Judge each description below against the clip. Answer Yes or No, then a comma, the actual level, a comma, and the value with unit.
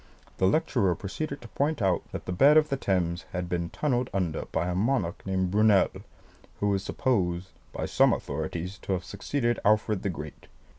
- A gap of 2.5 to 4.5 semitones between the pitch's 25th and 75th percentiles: No, average, 5.0 semitones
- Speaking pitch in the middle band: No, very low, 95 Hz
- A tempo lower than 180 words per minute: No, average, 185 wpm